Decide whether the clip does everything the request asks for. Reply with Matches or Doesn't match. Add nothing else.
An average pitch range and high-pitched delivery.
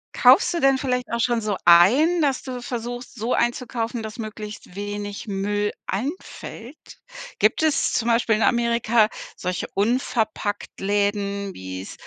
Matches